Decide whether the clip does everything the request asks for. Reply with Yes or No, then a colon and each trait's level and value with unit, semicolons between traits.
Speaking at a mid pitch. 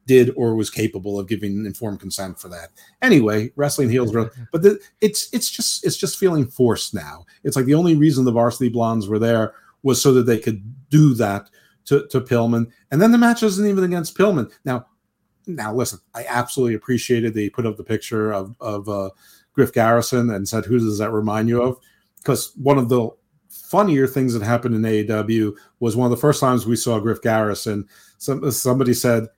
No: low, 120 Hz